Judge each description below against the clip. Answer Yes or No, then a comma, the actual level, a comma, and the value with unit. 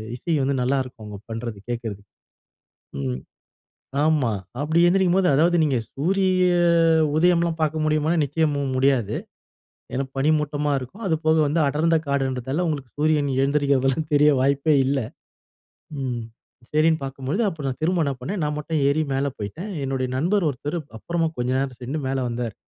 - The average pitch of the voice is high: No, medium, 145 Hz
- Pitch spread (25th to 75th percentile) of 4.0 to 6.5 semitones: No, average, 3.4 semitones